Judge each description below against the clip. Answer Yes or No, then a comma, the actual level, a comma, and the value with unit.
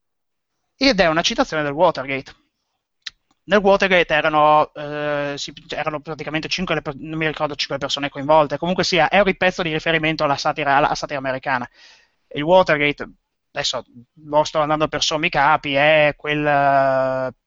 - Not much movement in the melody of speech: Yes, narrow, 2.0 semitones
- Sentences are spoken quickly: No, average, 155 wpm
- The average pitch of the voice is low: No, medium, 150 Hz